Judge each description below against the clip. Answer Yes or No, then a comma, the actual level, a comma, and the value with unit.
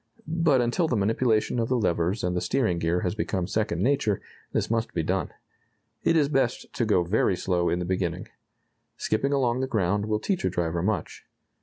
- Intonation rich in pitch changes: Yes, wide, 5.8 semitones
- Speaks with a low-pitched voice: Yes, low, 105 Hz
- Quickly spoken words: No, average, 195 wpm